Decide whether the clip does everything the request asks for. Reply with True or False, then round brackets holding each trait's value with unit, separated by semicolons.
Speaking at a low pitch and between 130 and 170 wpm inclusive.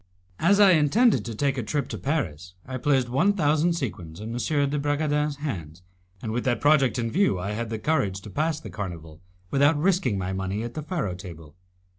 False (130 Hz; 205 wpm)